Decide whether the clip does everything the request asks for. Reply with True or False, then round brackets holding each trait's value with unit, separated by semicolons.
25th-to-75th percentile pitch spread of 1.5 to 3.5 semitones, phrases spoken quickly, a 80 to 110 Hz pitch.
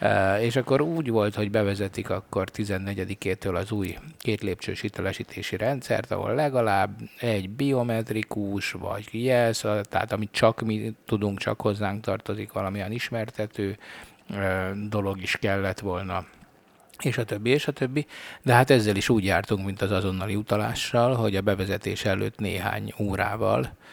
False (2.8 semitones; 140 wpm; 105 Hz)